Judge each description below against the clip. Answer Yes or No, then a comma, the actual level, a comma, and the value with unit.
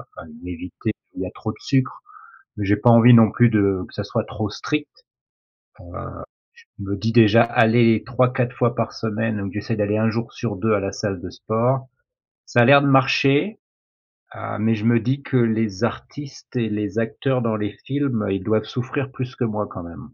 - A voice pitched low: Yes, low, 115 Hz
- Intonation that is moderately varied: Yes, average, 3.2 semitones